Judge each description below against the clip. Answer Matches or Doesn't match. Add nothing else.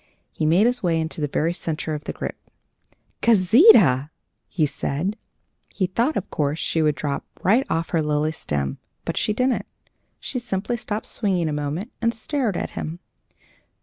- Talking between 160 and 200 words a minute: Matches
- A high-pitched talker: Doesn't match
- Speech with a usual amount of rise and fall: Doesn't match